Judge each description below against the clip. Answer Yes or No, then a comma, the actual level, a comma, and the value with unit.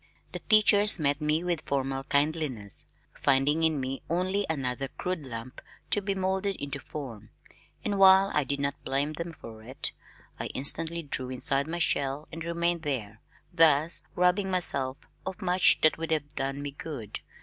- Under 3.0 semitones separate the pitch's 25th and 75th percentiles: No, average, 4.3 semitones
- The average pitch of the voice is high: No, medium, 150 Hz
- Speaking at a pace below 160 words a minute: No, average, 165 wpm